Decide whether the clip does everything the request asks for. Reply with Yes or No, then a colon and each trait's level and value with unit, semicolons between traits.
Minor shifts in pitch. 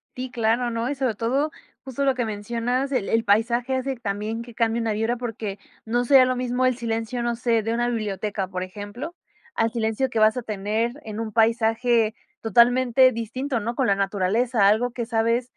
Yes: narrow, 2.2 semitones